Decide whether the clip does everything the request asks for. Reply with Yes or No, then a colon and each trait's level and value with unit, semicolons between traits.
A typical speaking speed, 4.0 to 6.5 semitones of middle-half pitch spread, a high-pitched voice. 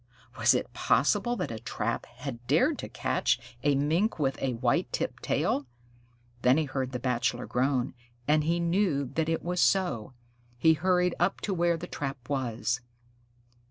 No: average, 165 wpm; wide, 5.4 semitones; medium, 140 Hz